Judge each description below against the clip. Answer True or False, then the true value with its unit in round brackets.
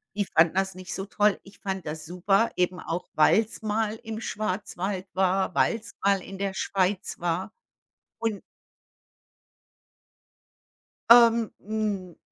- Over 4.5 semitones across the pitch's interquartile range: False (2.7 semitones)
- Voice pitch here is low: False (195 Hz)